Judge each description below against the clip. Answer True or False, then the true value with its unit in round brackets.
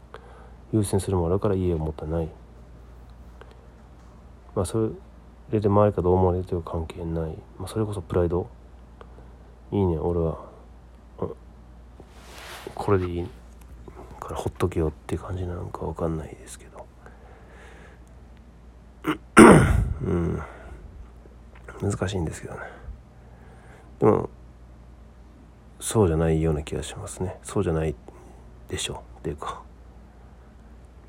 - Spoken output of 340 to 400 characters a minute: False (230 characters per minute)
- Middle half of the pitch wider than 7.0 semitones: False (6.6 semitones)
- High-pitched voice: False (75 Hz)